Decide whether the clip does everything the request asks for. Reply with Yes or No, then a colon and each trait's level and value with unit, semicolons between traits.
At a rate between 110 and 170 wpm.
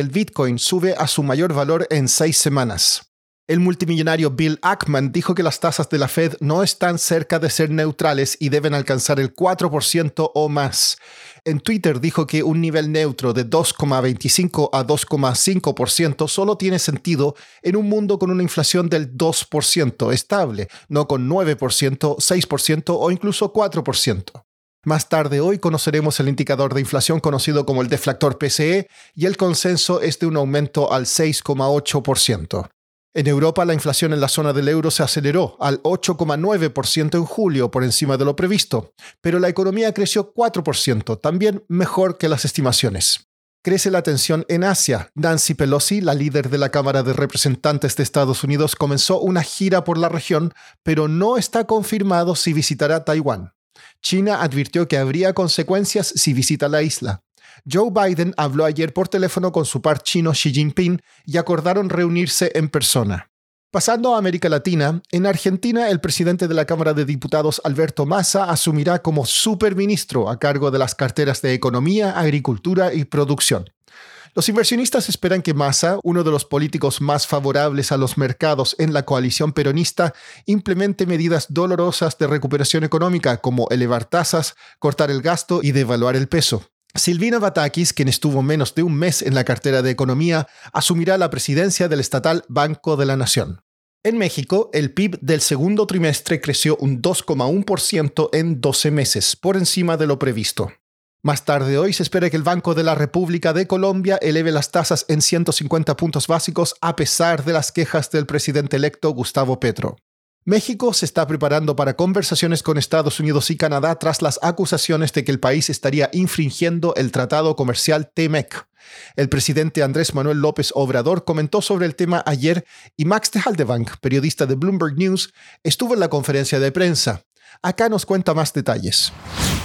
Yes: average, 165 wpm